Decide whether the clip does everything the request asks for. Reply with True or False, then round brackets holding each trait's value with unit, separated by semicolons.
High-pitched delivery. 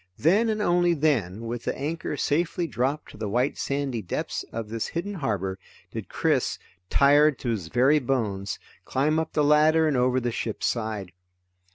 False (135 Hz)